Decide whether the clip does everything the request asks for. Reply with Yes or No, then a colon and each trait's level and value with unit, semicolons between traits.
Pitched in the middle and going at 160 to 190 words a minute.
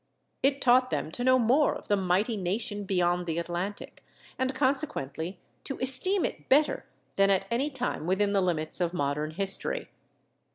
No: high, 200 Hz; average, 165 wpm